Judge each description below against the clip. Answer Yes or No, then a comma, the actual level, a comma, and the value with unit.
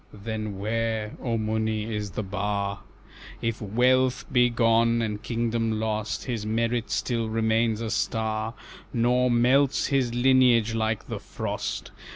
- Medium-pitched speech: No, low, 115 Hz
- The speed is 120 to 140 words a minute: Yes, slow, 135 wpm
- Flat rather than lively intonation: Yes, narrow, 1.6 semitones